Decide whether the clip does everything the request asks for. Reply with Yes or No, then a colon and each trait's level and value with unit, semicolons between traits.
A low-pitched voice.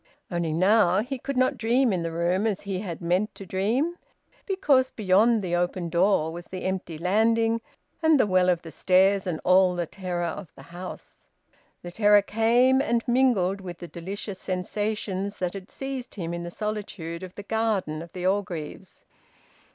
No: high, 190 Hz